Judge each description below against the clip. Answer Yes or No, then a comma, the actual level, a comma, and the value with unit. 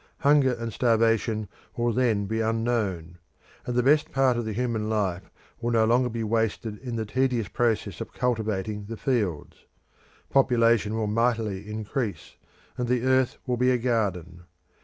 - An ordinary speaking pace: Yes, average, 160 wpm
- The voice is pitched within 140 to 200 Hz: No, low, 115 Hz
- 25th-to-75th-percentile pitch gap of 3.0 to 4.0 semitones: No, narrow, 2.6 semitones